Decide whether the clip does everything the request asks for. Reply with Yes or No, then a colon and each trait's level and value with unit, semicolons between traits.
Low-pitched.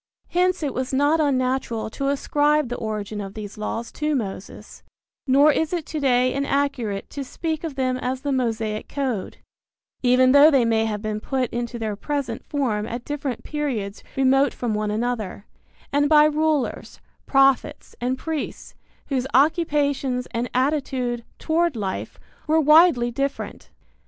No: very high, 260 Hz